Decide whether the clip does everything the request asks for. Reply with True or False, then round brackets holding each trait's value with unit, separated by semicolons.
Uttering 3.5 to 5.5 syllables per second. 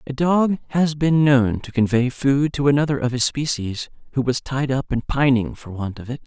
True (5.0 syllables/s)